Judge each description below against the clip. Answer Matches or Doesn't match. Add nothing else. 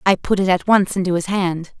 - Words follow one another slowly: Doesn't match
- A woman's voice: Matches